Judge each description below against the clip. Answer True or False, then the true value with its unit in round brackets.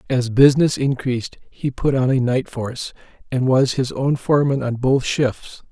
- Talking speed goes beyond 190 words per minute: False (180 wpm)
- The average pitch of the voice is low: True (130 Hz)